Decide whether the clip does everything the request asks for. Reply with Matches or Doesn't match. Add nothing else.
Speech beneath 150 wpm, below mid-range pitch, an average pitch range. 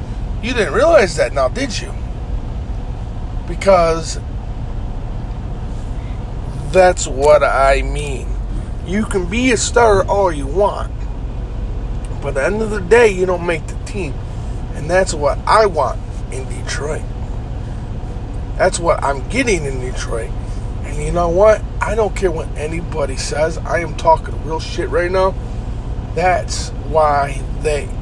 Doesn't match